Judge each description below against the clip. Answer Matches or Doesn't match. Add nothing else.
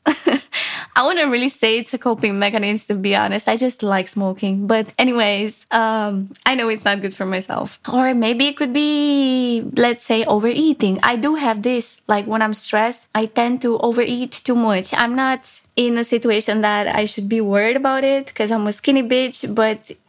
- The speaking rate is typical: Matches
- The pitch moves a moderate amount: Matches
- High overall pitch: Matches